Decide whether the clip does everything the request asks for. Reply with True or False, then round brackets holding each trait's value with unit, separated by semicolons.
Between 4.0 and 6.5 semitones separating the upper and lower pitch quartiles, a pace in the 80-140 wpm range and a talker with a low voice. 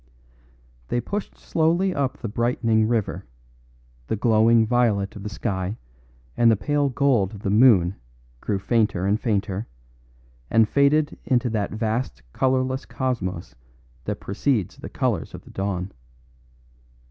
True (4.3 semitones; 135 wpm; 115 Hz)